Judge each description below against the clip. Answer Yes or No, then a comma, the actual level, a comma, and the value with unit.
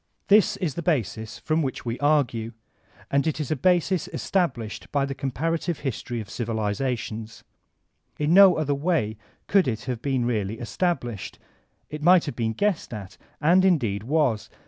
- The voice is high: No, medium, 140 Hz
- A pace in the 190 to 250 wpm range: No, average, 160 wpm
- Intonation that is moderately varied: No, wide, 6.5 semitones